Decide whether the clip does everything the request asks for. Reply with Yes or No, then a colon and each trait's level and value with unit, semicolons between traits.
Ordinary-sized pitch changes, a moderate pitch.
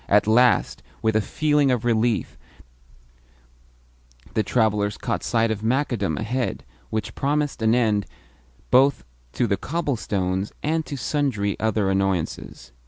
No: average, 4.3 semitones; low, 110 Hz